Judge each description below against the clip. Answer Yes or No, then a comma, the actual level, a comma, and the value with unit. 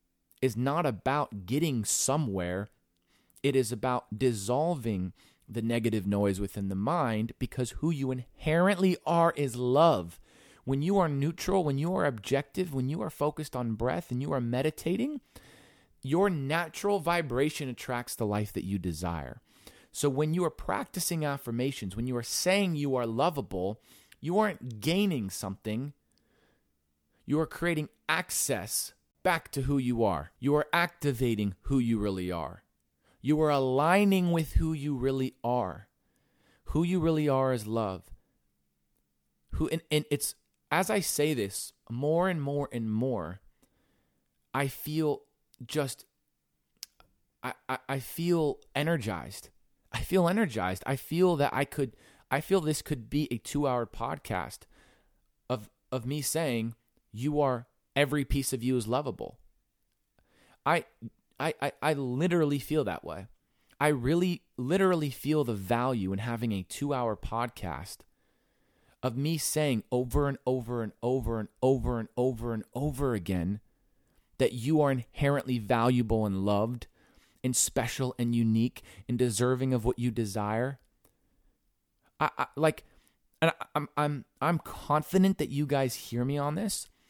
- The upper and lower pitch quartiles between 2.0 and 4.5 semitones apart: No, average, 5.0 semitones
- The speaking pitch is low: Yes, low, 130 Hz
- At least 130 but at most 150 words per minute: Yes, average, 145 wpm